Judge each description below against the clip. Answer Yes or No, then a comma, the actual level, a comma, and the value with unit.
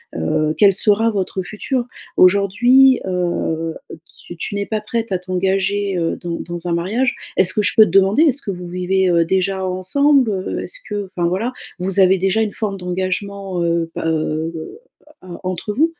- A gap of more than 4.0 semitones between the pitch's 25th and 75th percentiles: No, average, 2.9 semitones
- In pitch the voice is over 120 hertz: Yes, high, 190 Hz